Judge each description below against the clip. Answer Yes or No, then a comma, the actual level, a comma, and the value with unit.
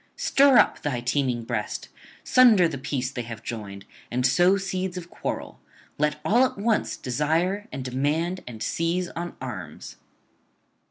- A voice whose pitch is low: No, medium, 150 Hz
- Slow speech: No, average, 150 wpm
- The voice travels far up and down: Yes, wide, 6.9 semitones